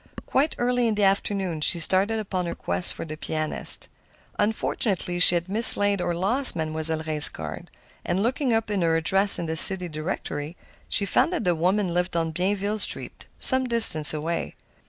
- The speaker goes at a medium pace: Yes, average, 175 wpm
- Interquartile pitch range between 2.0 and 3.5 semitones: No, average, 4.4 semitones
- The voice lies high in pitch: No, medium, 180 Hz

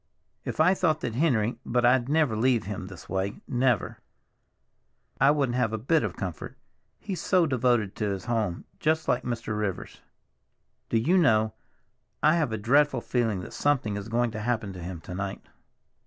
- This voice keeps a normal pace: Yes, average, 170 wpm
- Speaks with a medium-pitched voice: No, low, 120 Hz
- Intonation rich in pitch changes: No, average, 4.8 semitones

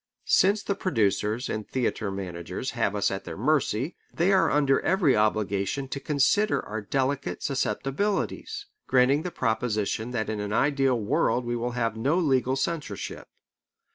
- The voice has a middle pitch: No, low, 125 Hz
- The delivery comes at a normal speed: Yes, average, 150 wpm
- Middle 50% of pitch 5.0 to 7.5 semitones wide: Yes, wide, 5.4 semitones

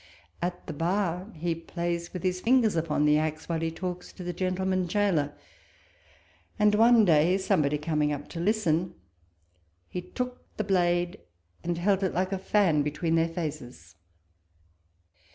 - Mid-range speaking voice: Yes, medium, 175 Hz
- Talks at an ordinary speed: Yes, average, 155 wpm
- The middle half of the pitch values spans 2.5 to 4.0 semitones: Yes, average, 2.8 semitones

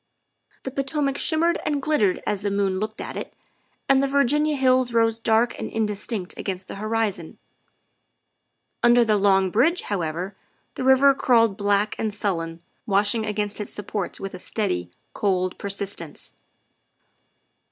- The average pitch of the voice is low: No, high, 210 Hz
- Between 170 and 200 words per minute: No, average, 150 wpm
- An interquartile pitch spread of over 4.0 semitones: Yes, average, 4.6 semitones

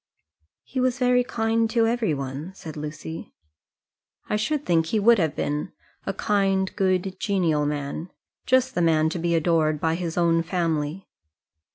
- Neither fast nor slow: Yes, average, 160 wpm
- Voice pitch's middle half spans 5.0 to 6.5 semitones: Yes, wide, 5.6 semitones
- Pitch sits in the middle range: Yes, medium, 175 Hz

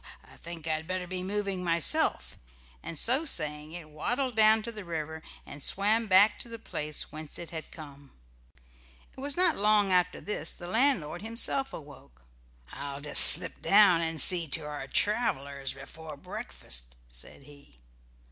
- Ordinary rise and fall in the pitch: No, wide, 5.9 semitones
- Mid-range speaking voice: Yes, medium, 170 Hz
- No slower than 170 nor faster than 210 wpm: No, average, 160 wpm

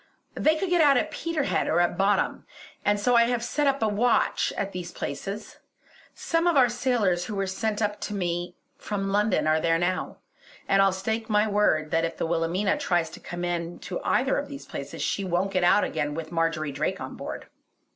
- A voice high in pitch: Yes, high, 195 Hz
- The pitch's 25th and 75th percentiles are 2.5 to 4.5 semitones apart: No, average, 5.1 semitones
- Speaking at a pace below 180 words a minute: No, fast, 205 wpm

